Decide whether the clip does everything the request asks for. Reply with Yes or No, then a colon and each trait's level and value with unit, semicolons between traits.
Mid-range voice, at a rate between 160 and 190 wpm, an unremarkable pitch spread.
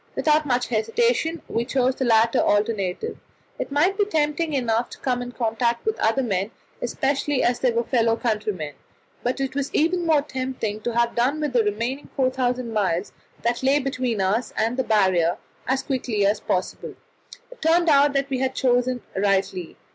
No: high, 245 Hz; average, 180 wpm; average, 3.9 semitones